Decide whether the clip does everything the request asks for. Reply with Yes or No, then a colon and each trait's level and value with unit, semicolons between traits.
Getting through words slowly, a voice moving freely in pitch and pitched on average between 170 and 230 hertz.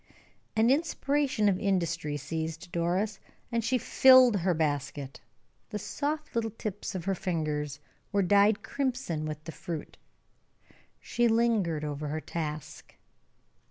Yes: slow, 125 wpm; wide, 6.6 semitones; high, 190 Hz